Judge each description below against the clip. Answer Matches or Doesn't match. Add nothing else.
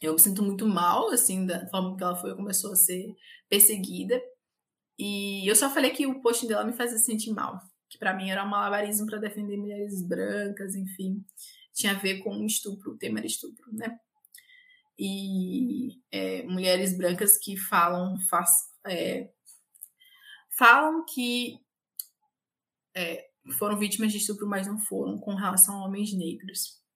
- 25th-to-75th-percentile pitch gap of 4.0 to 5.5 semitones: Doesn't match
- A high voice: Matches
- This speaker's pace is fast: Doesn't match